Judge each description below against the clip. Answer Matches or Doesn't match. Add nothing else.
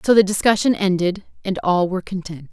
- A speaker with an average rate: Matches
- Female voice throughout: Matches